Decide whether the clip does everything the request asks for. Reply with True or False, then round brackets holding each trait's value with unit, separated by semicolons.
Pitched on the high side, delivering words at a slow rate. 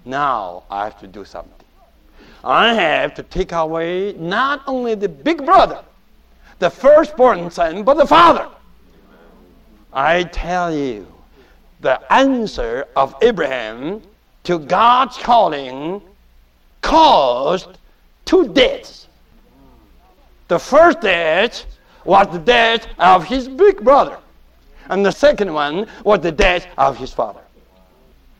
True (210 Hz; 115 wpm)